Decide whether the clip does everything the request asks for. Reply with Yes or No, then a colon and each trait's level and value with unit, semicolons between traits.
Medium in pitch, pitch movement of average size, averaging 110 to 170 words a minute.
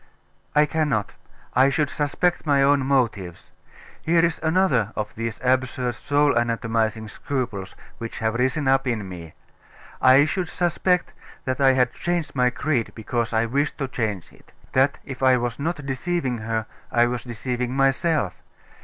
No: low, 130 Hz; average, 3.9 semitones; average, 155 wpm